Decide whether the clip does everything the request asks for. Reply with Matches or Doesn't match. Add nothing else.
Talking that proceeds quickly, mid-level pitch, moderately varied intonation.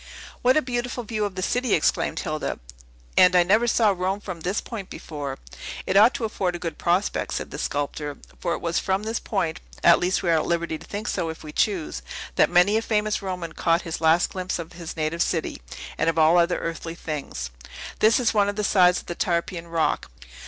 Matches